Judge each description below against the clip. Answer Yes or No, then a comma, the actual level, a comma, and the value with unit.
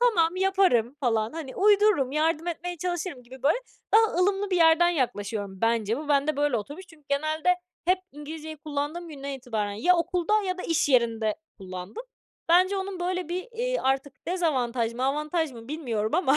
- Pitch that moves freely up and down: Yes, wide, 6.1 semitones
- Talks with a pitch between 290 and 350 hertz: Yes, very high, 310 Hz